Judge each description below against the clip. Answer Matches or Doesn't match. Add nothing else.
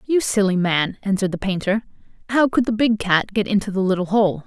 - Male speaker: Doesn't match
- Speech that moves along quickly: Matches